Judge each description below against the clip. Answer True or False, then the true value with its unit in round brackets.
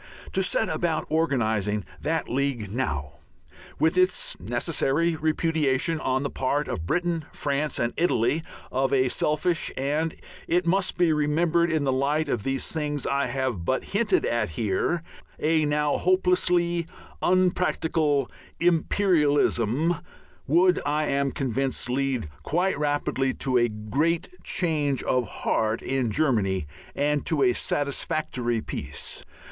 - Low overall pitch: False (145 Hz)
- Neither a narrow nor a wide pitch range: True (4.2 semitones)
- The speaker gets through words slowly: True (130 wpm)